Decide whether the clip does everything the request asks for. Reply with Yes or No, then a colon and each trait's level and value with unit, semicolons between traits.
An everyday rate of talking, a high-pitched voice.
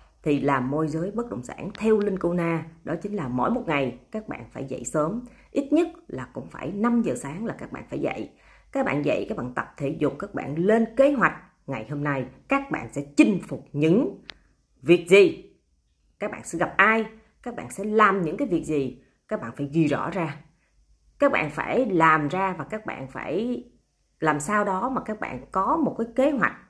No: average, 220 wpm; medium, 175 Hz